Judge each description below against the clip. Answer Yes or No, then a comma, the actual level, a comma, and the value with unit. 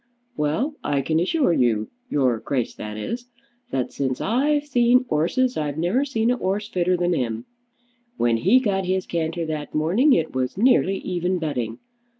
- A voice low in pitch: No, medium, 175 Hz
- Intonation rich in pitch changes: Yes, wide, 8.8 semitones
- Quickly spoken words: No, average, 165 wpm